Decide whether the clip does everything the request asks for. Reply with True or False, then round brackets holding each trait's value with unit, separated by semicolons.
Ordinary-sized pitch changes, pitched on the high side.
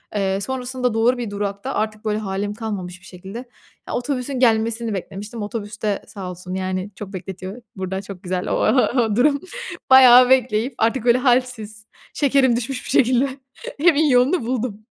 True (4.0 semitones; 225 Hz)